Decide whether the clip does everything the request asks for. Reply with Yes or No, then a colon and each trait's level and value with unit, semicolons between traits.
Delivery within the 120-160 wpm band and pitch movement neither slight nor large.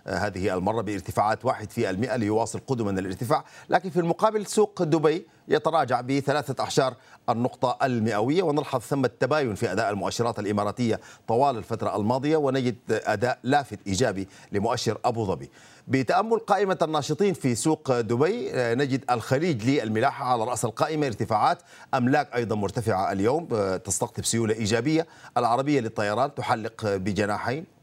Yes: average, 130 wpm; average, 4.6 semitones